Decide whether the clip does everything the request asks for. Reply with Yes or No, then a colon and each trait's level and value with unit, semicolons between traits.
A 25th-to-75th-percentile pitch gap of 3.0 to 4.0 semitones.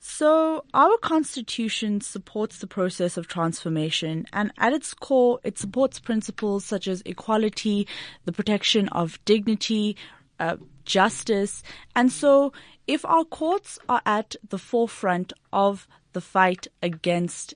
No: average, 4.7 semitones